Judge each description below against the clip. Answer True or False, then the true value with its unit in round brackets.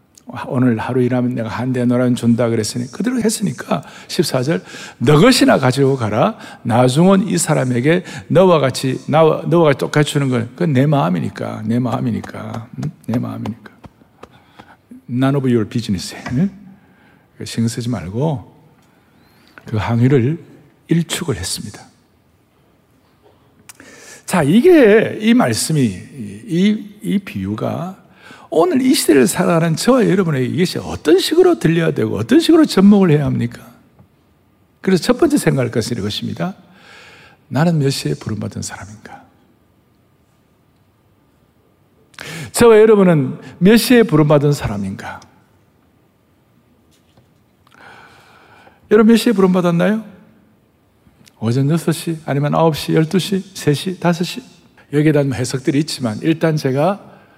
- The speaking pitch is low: False (150 Hz)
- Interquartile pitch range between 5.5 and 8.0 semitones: True (7.5 semitones)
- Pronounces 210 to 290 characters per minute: True (255 characters per minute)